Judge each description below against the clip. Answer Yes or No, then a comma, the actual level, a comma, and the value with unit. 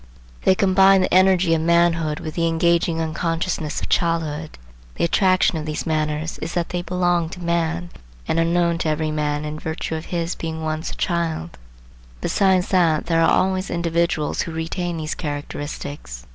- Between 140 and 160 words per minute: No, average, 175 wpm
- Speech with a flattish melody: Yes, narrow, 1.9 semitones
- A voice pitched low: No, medium, 165 Hz